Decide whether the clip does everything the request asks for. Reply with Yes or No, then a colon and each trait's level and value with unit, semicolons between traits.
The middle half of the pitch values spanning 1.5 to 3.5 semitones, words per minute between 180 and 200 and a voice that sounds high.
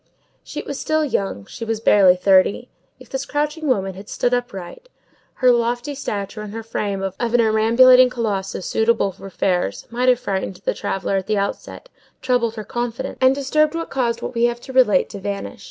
No: average, 4.3 semitones; average, 190 wpm; high, 230 Hz